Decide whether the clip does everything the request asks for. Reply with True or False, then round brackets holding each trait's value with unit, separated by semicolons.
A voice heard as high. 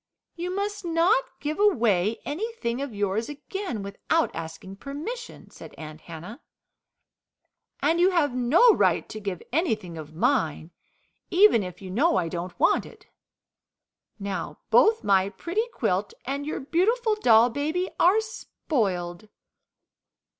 True (270 Hz)